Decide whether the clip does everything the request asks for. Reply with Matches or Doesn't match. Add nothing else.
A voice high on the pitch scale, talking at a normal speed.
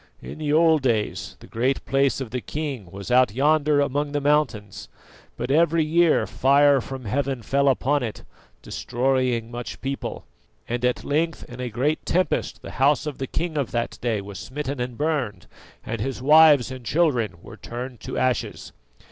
Doesn't match